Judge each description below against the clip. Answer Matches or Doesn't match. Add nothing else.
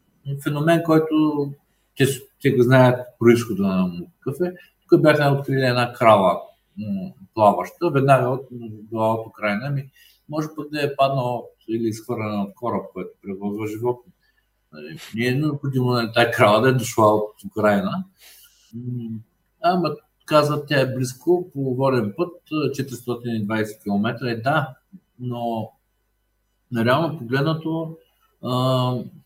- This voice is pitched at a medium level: Doesn't match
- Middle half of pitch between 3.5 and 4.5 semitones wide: Doesn't match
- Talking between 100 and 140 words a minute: Matches